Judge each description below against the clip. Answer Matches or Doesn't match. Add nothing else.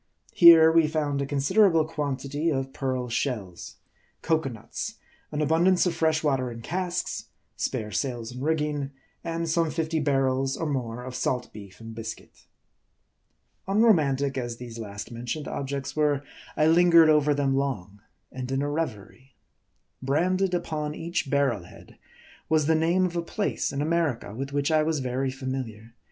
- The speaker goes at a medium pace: Matches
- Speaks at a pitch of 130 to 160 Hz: Matches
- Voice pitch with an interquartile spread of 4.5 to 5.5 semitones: Doesn't match